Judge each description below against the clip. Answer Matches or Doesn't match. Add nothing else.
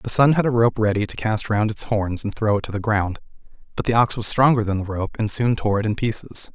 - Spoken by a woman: Doesn't match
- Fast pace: Matches